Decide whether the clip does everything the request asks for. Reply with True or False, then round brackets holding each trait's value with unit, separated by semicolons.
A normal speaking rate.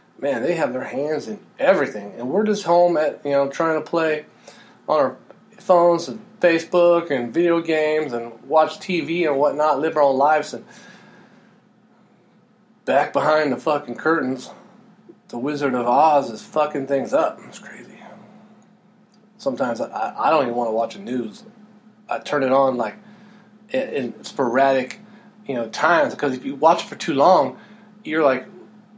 True (165 wpm)